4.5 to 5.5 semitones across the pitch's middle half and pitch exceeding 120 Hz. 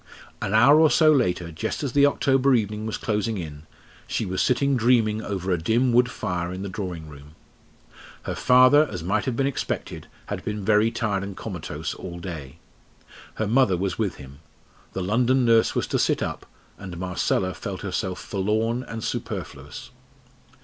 No: average, 5.2 semitones; low, 105 Hz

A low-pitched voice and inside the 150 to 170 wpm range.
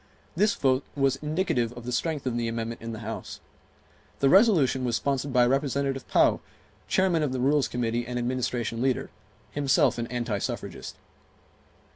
Yes: low, 130 Hz; average, 160 wpm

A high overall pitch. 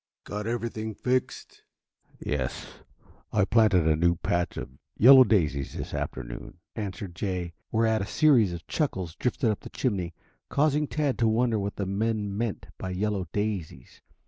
No: low, 105 Hz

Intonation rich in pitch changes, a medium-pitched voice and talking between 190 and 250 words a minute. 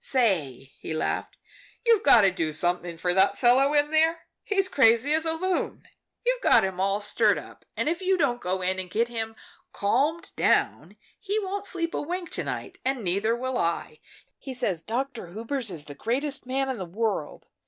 No: wide, 8.2 semitones; high, 240 Hz; average, 195 wpm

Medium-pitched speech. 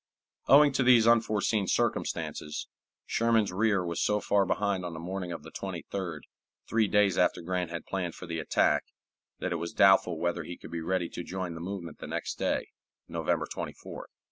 No: very low, 95 Hz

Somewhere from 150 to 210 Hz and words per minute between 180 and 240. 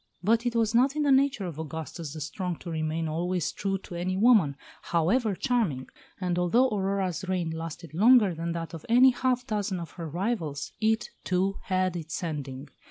Yes: medium, 185 Hz; average, 185 wpm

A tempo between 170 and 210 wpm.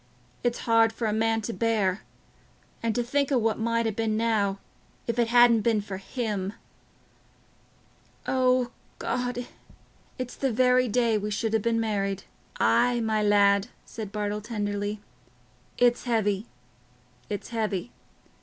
No: slow, 135 wpm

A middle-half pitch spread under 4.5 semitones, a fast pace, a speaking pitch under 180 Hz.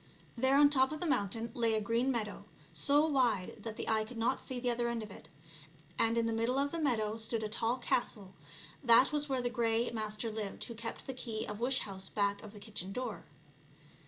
No: average, 2.8 semitones; fast, 235 wpm; high, 230 Hz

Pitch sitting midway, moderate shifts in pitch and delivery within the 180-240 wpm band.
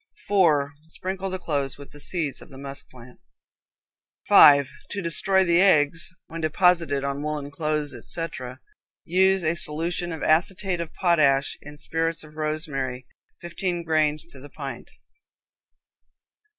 No: medium, 155 Hz; average, 3.3 semitones; slow, 135 wpm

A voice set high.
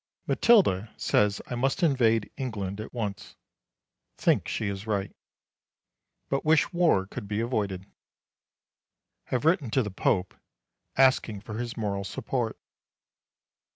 No: low, 110 Hz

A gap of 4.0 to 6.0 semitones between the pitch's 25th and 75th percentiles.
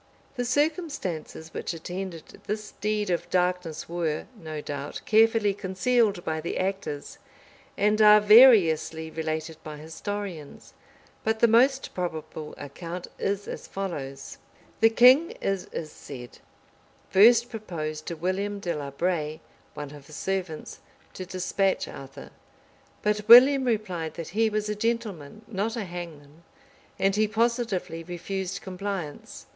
Yes: average, 5.0 semitones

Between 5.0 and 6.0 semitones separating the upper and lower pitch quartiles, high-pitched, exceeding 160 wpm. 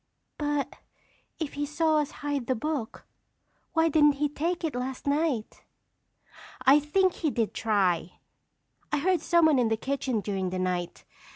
No: wide, 5.6 semitones; very high, 285 Hz; average, 155 wpm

